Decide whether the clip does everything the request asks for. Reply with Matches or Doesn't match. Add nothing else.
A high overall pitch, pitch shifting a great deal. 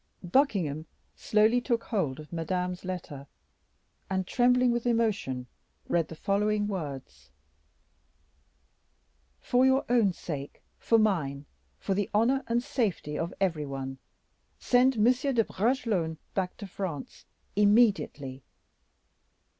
Matches